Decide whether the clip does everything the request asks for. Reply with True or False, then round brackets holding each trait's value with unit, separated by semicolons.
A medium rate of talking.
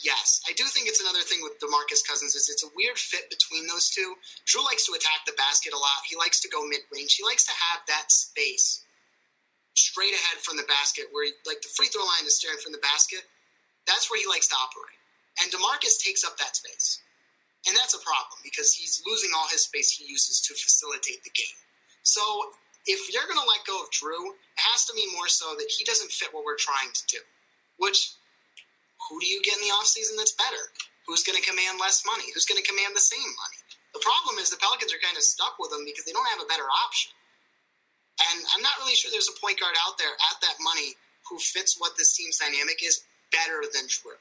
False (230 wpm)